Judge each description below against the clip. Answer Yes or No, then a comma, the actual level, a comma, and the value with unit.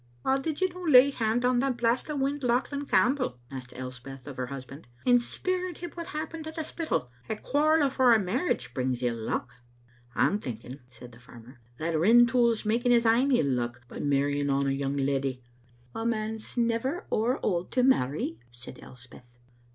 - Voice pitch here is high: Yes, high, 220 Hz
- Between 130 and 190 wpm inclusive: No, average, 200 wpm